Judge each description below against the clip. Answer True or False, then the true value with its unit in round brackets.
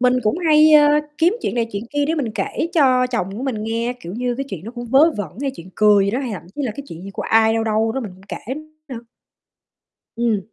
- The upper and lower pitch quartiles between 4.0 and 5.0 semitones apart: True (4.4 semitones)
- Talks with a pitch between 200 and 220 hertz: False (235 Hz)